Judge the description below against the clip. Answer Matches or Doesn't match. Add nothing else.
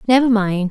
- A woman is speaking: Matches